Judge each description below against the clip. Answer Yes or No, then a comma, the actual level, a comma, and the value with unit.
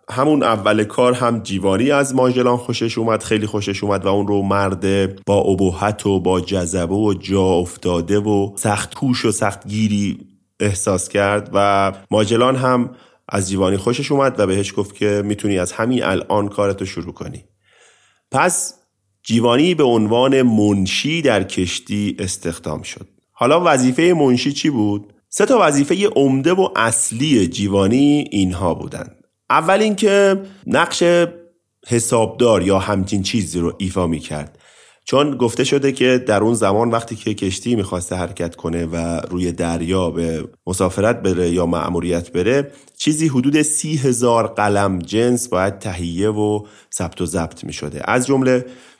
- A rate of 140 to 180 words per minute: Yes, average, 150 wpm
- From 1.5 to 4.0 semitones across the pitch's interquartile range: No, average, 4.8 semitones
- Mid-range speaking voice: No, low, 105 Hz